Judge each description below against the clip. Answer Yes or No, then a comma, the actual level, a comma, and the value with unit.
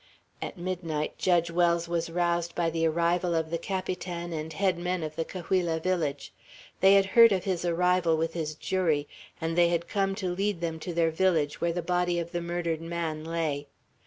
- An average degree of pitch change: No, narrow, 1.7 semitones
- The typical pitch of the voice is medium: Yes, medium, 170 Hz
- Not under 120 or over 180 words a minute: No, average, 195 wpm